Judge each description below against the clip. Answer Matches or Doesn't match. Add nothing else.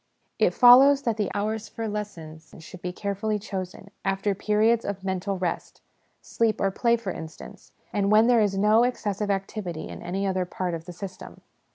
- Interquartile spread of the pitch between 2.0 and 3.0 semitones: Matches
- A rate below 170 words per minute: Doesn't match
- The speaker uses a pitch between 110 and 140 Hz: Doesn't match